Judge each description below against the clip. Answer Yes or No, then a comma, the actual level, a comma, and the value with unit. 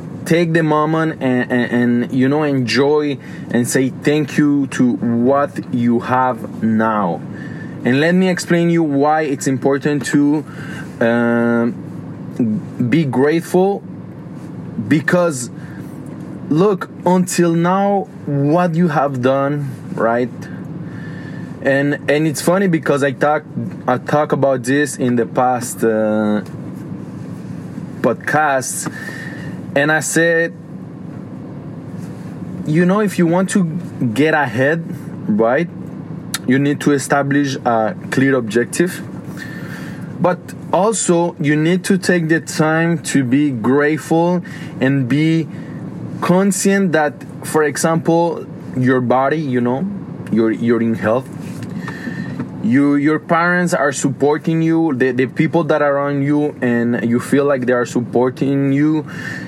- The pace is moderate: No, slow, 120 wpm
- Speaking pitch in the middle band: Yes, medium, 150 Hz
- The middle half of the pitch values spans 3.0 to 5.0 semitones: Yes, average, 4.2 semitones